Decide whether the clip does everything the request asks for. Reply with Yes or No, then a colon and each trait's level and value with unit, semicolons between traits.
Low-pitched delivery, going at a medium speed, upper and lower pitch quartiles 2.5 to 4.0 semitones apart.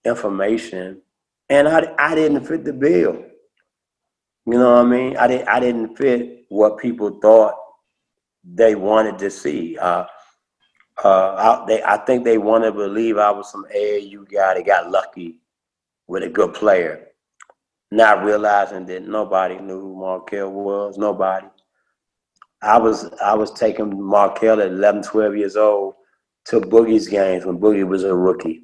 Yes: low, 105 Hz; average, 155 wpm; average, 2.9 semitones